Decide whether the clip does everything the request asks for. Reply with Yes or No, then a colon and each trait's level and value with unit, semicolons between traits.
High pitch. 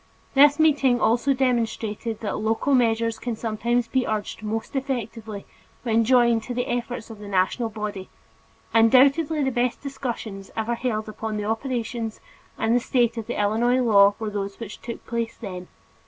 Yes: high, 230 Hz